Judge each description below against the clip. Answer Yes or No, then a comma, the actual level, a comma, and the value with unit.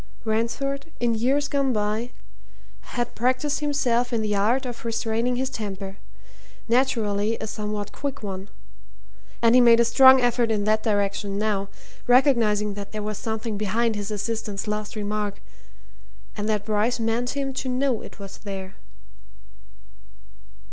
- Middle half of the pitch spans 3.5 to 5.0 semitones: No, average, 2.9 semitones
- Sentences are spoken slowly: No, average, 145 wpm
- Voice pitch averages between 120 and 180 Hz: No, high, 225 Hz